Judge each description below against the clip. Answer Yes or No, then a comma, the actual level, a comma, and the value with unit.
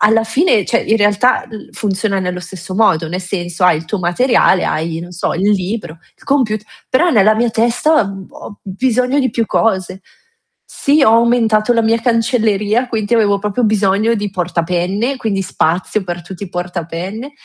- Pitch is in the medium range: No, high, 210 Hz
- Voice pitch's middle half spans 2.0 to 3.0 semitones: No, average, 4.0 semitones